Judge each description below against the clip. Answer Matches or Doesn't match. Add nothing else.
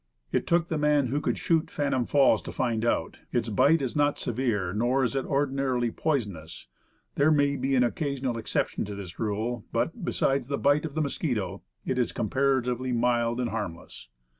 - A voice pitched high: Doesn't match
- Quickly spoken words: Doesn't match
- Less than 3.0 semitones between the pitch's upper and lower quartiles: Doesn't match